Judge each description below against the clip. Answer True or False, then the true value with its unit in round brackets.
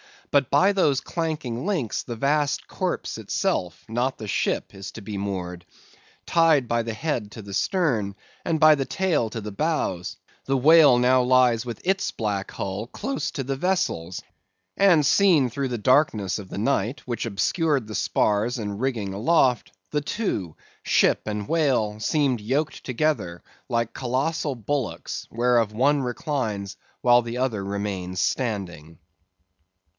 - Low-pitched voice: True (120 Hz)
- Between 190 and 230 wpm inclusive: False (150 wpm)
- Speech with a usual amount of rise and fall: False (5.8 semitones)